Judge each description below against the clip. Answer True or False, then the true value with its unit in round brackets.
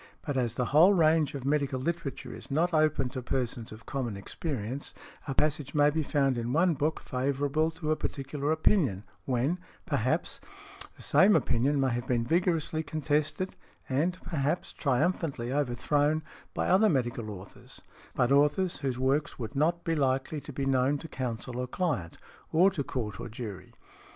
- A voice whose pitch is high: False (140 Hz)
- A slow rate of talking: False (165 wpm)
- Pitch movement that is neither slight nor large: True (3.8 semitones)